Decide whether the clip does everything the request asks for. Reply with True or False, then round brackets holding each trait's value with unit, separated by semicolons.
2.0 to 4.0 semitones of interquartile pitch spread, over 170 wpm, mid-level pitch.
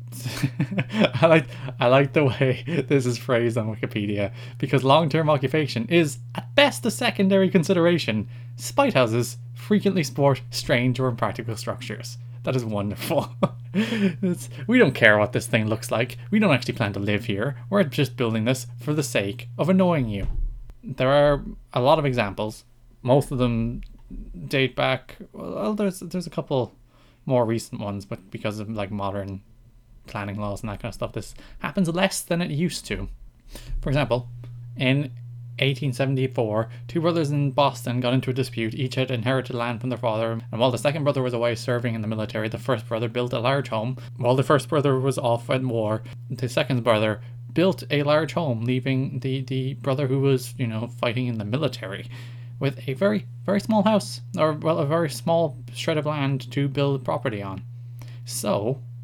False (3.4 semitones; 180 wpm; 125 Hz)